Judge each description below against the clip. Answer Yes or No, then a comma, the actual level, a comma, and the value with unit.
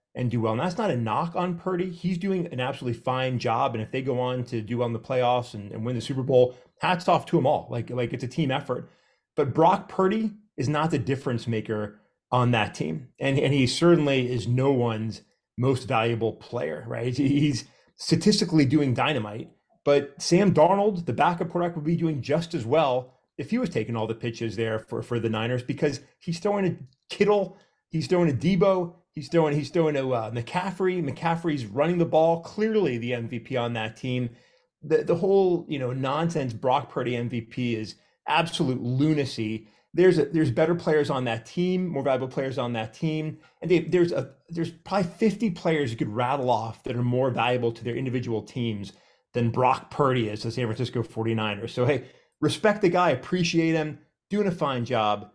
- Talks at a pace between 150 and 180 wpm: No, average, 200 wpm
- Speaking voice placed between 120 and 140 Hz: Yes, low, 135 Hz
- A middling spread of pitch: No, wide, 5.7 semitones